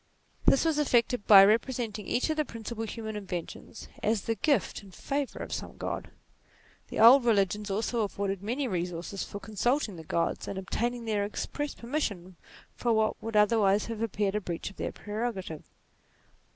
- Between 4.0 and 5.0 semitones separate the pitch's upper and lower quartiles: No, average, 3.3 semitones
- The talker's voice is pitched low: No, high, 215 Hz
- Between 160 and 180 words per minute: Yes, average, 170 wpm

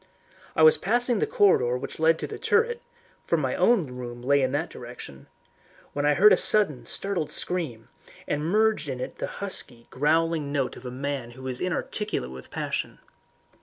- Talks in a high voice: No, medium, 150 Hz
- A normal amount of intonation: No, wide, 7.7 semitones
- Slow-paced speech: No, average, 180 wpm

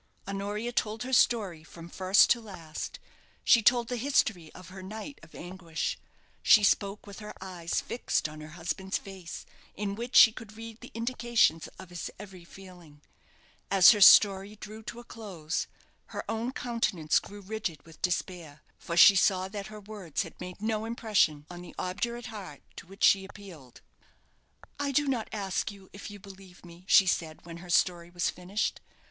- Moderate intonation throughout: Yes, average, 3.8 semitones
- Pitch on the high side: Yes, high, 195 Hz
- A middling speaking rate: Yes, average, 175 wpm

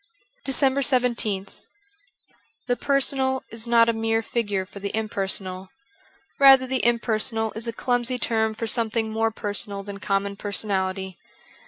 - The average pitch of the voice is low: No, high, 225 Hz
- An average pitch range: Yes, average, 3.3 semitones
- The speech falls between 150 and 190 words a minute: No, average, 140 wpm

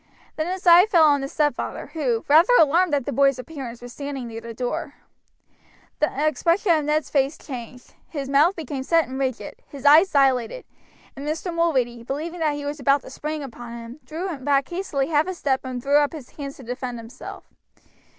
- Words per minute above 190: Yes, average, 200 wpm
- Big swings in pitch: No, average, 3.5 semitones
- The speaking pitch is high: Yes, very high, 285 Hz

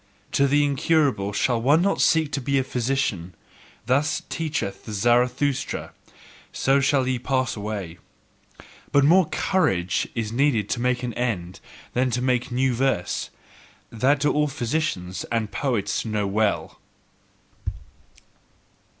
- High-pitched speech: No, low, 125 Hz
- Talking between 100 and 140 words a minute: Yes, slow, 135 wpm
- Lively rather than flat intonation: No, average, 4.5 semitones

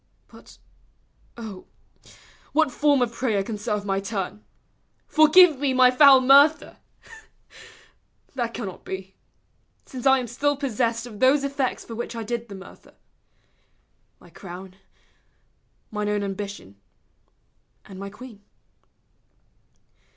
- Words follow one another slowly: Yes, slow, 125 wpm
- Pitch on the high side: Yes, high, 235 Hz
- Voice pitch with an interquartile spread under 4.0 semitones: No, average, 4.8 semitones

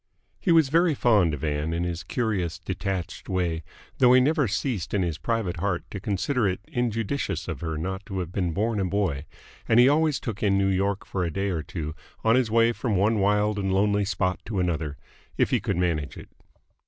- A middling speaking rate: No, fast, 215 wpm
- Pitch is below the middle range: Yes, low, 100 Hz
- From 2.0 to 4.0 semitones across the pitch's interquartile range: No, average, 4.5 semitones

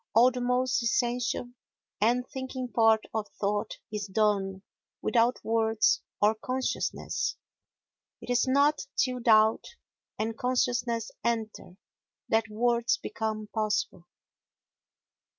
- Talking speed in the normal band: No, slow, 105 wpm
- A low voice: No, high, 230 Hz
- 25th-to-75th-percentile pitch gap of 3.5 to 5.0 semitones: No, narrow, 2.4 semitones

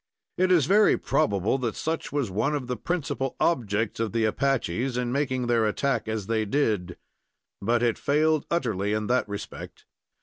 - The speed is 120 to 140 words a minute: No, average, 170 wpm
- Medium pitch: No, low, 120 Hz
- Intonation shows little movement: No, average, 4.7 semitones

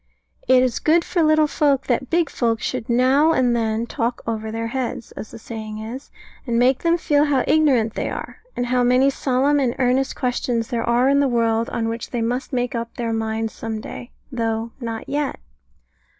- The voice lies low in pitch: No, high, 245 Hz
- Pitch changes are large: No, average, 2.9 semitones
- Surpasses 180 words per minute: Yes, average, 200 wpm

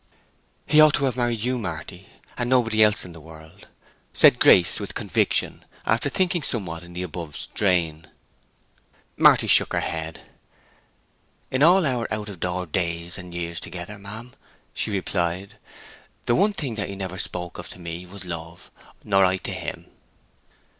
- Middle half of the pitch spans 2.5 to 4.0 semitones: No, average, 5.2 semitones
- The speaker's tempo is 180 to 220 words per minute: No, average, 160 wpm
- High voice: No, very low, 95 Hz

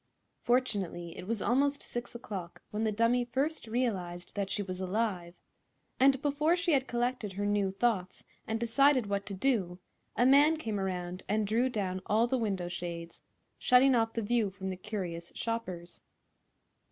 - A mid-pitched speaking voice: No, high, 215 Hz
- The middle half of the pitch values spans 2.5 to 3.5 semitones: No, average, 4.7 semitones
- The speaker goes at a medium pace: Yes, average, 165 wpm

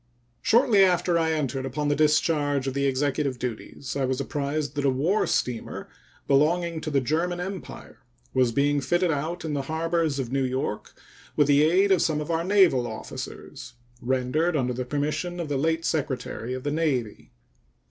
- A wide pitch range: No, average, 3.8 semitones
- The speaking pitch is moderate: Yes, medium, 145 Hz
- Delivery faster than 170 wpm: Yes, average, 180 wpm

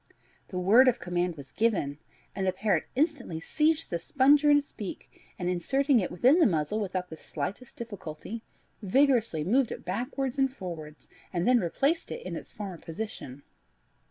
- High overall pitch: Yes, high, 210 Hz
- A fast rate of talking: No, average, 170 wpm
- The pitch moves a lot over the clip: Yes, wide, 7.3 semitones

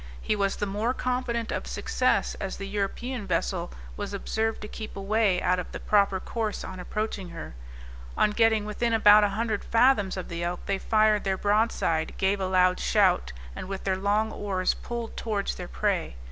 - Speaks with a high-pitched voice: Yes, high, 205 Hz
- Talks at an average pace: Yes, average, 190 wpm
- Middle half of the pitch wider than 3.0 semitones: No, narrow, 2.6 semitones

